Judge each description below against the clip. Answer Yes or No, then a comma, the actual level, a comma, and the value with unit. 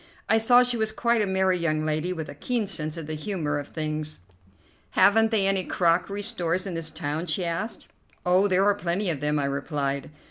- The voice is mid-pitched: Yes, medium, 175 Hz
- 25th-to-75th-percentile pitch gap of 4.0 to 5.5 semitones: Yes, average, 4.8 semitones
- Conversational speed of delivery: No, fast, 210 wpm